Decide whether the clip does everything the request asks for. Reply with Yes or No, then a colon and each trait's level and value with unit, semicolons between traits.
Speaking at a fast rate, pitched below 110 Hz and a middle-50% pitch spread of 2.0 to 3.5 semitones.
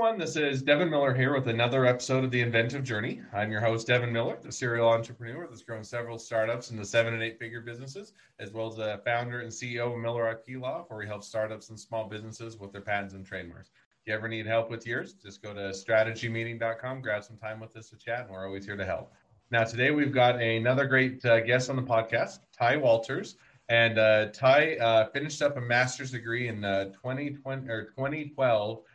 No: fast, 215 wpm; low, 115 Hz; narrow, 2.5 semitones